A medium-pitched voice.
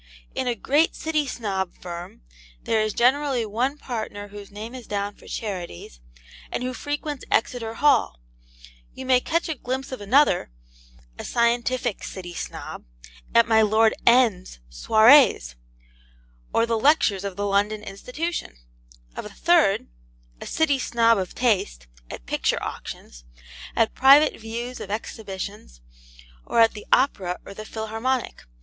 No: high, 225 Hz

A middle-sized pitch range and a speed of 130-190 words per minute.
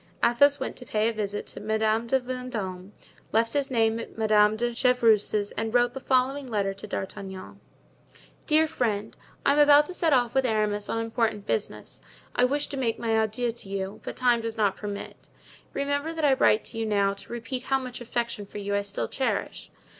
No: average, 3.5 semitones; average, 200 wpm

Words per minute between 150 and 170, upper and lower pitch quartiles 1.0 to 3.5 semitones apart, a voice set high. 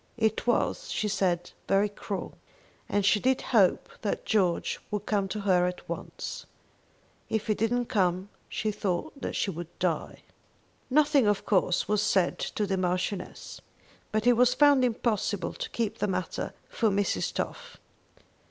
Yes: average, 155 wpm; average, 3.1 semitones; high, 205 Hz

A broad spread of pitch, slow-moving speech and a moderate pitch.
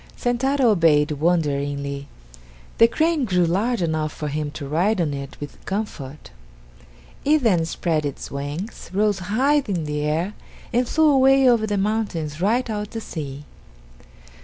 No: wide, 7.3 semitones; average, 150 wpm; medium, 180 Hz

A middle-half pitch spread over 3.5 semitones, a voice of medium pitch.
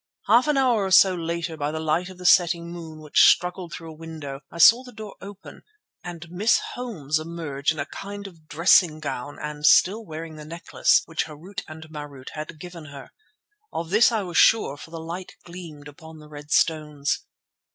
No: average, 3.2 semitones; medium, 165 Hz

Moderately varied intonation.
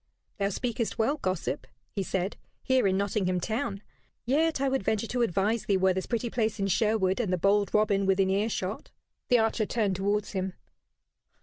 Yes: average, 3.0 semitones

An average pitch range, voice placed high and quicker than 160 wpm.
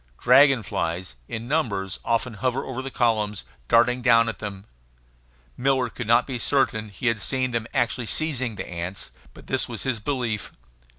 No: average, 3.4 semitones; low, 115 Hz; average, 170 wpm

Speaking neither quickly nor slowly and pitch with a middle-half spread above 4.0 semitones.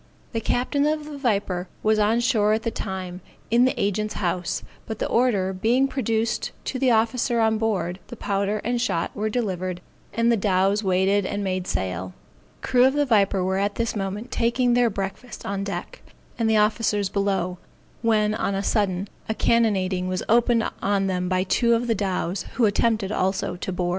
No: average, 190 wpm; average, 3.5 semitones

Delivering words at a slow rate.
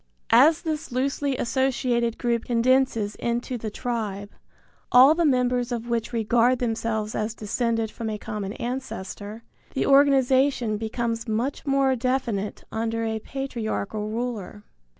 Yes: slow, 130 wpm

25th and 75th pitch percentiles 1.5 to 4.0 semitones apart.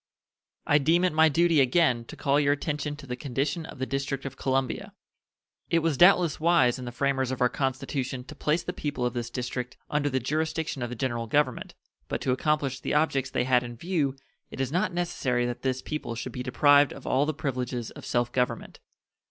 Yes: average, 3.3 semitones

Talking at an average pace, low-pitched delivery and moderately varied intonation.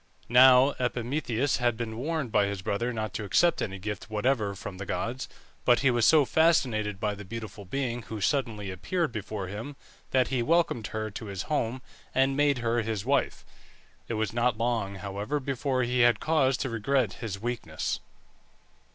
Yes: average, 175 wpm; low, 120 Hz; average, 3.8 semitones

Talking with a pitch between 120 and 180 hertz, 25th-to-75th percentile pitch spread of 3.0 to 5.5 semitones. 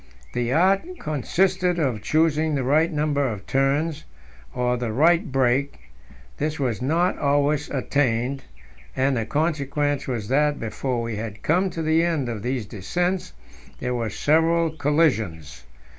Yes: medium, 140 Hz; average, 4.4 semitones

